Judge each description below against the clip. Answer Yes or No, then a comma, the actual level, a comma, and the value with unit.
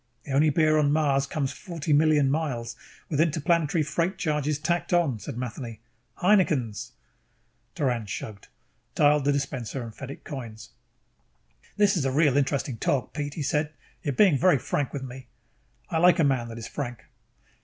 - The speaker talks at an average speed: Yes, average, 170 wpm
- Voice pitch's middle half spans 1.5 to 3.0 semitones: No, average, 3.4 semitones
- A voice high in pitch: No, medium, 145 Hz